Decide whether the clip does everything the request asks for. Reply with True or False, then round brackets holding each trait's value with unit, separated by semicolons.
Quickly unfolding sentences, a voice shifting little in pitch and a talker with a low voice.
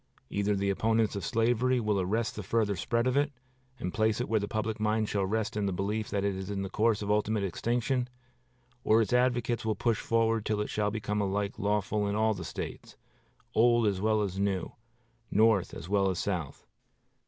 True (210 wpm; 2.0 semitones; 105 Hz)